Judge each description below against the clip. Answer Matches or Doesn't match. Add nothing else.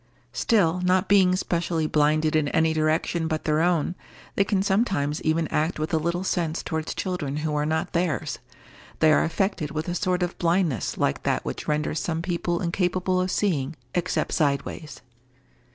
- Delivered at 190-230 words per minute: Doesn't match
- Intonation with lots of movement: Doesn't match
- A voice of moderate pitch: Matches